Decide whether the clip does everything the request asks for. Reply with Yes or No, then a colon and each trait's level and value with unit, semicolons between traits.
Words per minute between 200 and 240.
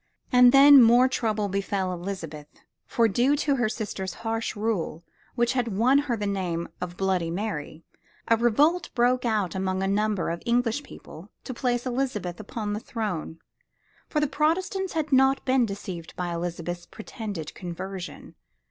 No: average, 160 wpm